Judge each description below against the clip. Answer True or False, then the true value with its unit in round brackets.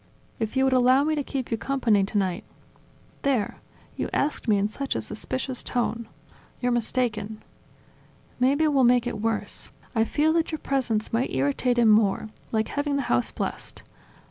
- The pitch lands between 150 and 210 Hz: False (245 Hz)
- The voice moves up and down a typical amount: True (4.0 semitones)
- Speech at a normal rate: True (175 wpm)